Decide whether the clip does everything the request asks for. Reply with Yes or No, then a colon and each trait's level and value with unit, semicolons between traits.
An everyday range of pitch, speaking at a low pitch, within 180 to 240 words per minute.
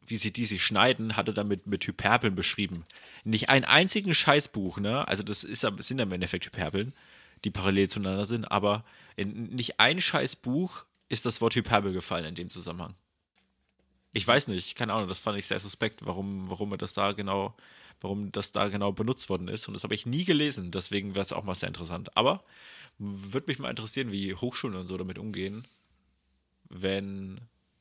Yes: average, 3.0 semitones; low, 100 Hz; fast, 190 wpm